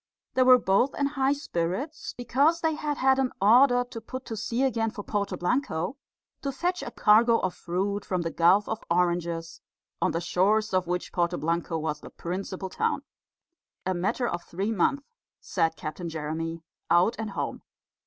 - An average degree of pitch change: No, wide, 6.6 semitones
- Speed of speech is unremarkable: Yes, average, 175 wpm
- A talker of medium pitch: No, high, 200 Hz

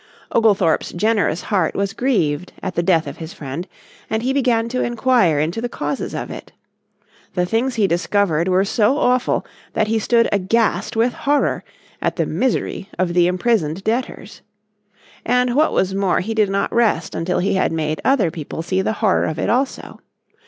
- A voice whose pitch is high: Yes, high, 200 Hz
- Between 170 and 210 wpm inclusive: Yes, average, 180 wpm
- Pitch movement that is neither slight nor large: Yes, average, 4.9 semitones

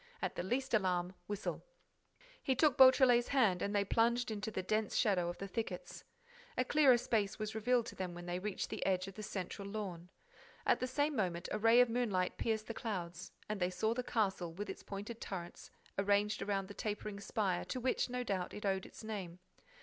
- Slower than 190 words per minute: No, fast, 205 wpm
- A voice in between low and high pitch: No, high, 210 Hz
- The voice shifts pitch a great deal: No, average, 3.9 semitones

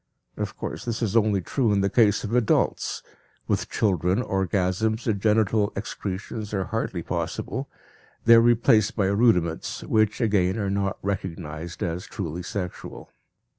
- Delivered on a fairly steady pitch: No, average, 3.2 semitones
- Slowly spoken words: No, average, 145 wpm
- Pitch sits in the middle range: No, low, 100 Hz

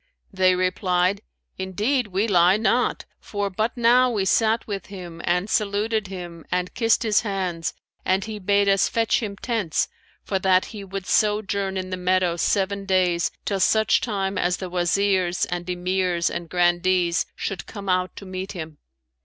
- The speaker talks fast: No, average, 165 wpm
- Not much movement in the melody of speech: Yes, narrow, 2.2 semitones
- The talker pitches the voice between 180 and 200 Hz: Yes, high, 190 Hz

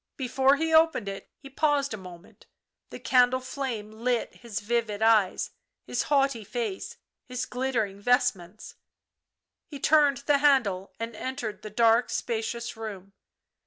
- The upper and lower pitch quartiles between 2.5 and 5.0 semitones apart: Yes, average, 4.0 semitones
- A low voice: No, high, 235 Hz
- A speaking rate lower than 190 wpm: Yes, slow, 135 wpm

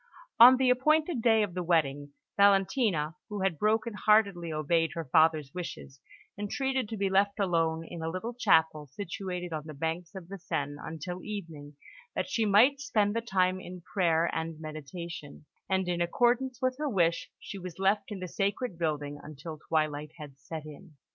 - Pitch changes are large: No, average, 4.5 semitones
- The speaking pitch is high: No, medium, 180 Hz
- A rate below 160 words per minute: No, average, 175 wpm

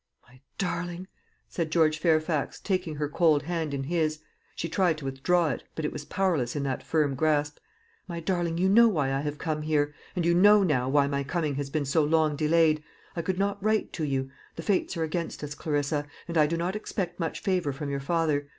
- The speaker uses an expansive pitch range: No, average, 3.1 semitones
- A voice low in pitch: No, medium, 155 Hz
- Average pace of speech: No, fast, 215 wpm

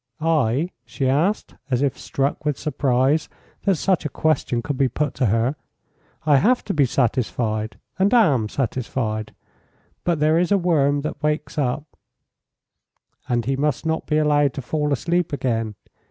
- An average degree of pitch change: Yes, average, 3.8 semitones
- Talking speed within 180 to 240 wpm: No, average, 165 wpm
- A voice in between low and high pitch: Yes, medium, 145 Hz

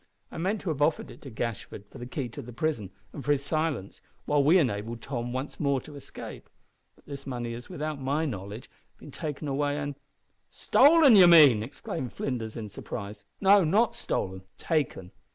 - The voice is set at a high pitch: No, medium, 140 Hz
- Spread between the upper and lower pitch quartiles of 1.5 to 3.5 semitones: No, average, 4.8 semitones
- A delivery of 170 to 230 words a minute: Yes, average, 190 wpm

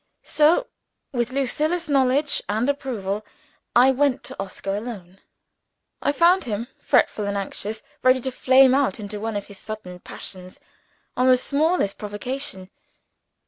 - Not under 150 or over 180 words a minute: No, average, 140 wpm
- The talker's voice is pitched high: Yes, high, 245 Hz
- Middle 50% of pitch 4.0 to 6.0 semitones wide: Yes, average, 5.2 semitones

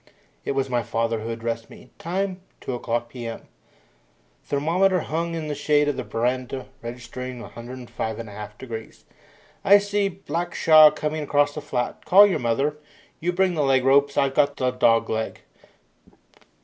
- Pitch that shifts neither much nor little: Yes, average, 5.0 semitones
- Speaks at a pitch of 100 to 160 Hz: Yes, low, 135 Hz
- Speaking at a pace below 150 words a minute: No, average, 155 wpm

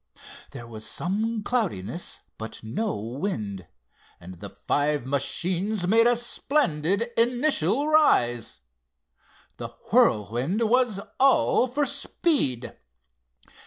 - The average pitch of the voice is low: No, high, 190 Hz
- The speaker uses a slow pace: Yes, slow, 95 wpm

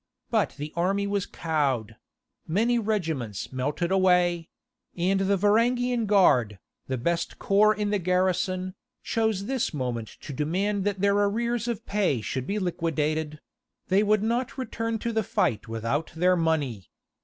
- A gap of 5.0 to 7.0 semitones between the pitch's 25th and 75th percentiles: Yes, wide, 5.5 semitones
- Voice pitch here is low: No, medium, 185 Hz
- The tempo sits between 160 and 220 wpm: No, average, 145 wpm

